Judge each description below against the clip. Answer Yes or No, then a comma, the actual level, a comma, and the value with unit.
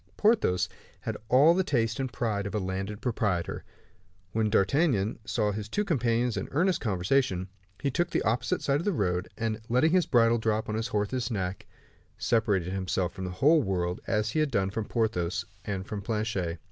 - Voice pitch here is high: No, low, 110 Hz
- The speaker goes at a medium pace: Yes, average, 185 wpm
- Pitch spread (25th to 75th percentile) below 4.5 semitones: No, average, 4.8 semitones